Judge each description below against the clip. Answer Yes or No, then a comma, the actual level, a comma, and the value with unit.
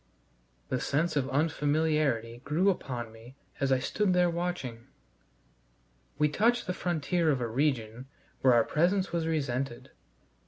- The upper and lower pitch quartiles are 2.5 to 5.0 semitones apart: No, wide, 5.4 semitones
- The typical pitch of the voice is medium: Yes, medium, 145 Hz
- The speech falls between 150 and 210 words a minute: No, slow, 135 wpm